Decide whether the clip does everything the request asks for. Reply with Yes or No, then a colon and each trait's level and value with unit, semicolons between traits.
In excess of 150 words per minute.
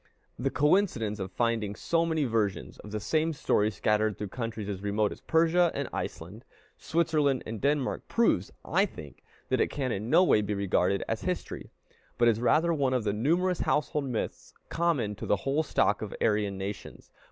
Yes: average, 185 wpm